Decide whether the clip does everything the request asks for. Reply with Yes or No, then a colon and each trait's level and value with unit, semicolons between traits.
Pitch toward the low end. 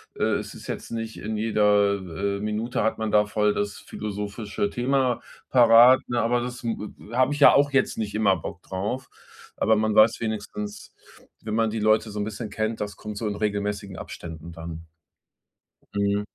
Yes: low, 105 Hz